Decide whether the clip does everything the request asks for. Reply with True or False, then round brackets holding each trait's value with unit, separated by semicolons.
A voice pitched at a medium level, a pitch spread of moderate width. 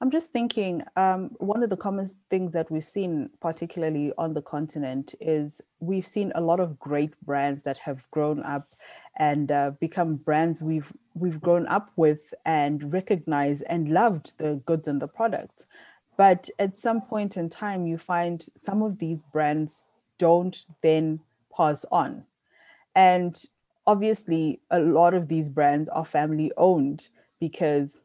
True (165 Hz; 3.9 semitones)